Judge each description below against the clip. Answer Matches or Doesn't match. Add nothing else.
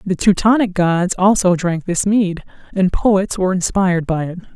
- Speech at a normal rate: Matches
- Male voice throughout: Doesn't match